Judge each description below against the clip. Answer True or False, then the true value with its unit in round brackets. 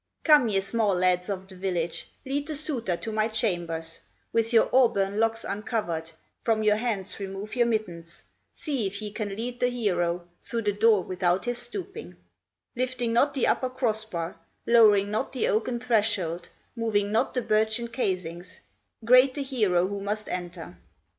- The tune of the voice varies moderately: True (4.2 semitones)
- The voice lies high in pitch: True (215 Hz)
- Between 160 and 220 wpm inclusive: True (165 wpm)